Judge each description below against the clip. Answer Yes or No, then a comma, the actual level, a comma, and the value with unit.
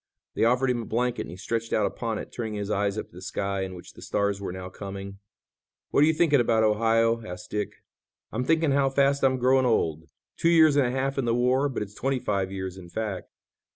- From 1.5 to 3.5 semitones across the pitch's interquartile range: No, average, 4.9 semitones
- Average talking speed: No, fast, 240 wpm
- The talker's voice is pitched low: Yes, low, 115 Hz